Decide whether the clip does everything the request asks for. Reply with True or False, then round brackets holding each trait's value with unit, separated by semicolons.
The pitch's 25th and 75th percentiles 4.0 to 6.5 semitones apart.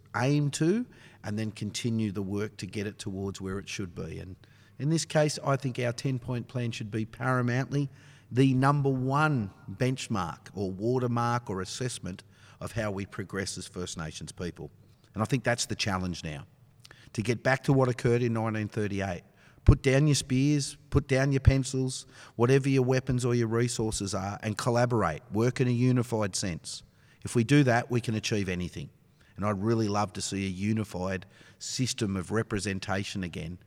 True (4.4 semitones)